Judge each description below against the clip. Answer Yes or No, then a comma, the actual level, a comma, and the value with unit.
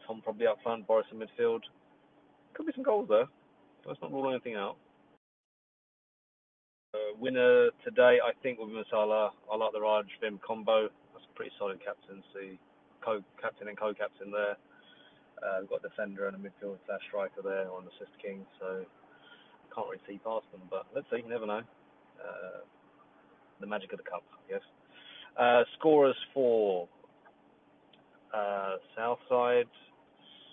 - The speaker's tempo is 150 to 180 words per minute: Yes, average, 160 wpm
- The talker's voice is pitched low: Yes, low, 110 Hz